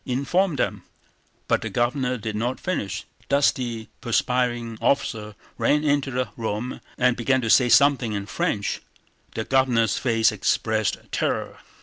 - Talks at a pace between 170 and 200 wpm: No, average, 140 wpm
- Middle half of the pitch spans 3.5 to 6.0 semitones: No, average, 2.9 semitones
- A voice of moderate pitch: No, low, 120 Hz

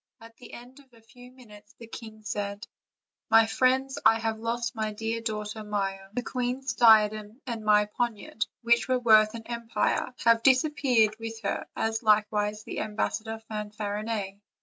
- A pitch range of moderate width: No, narrow, 2.0 semitones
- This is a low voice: No, high, 225 Hz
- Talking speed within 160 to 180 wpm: Yes, average, 165 wpm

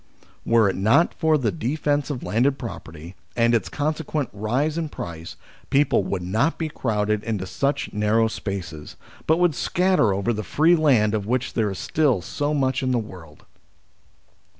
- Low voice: Yes, low, 120 Hz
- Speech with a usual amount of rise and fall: No, wide, 6.0 semitones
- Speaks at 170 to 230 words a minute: Yes, average, 175 wpm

